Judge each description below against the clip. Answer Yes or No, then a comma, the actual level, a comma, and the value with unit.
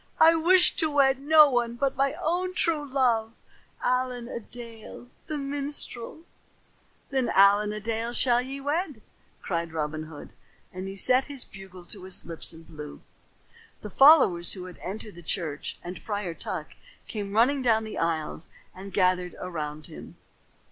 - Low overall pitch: No, high, 225 Hz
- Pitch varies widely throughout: Yes, wide, 7.0 semitones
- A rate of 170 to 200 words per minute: No, average, 155 wpm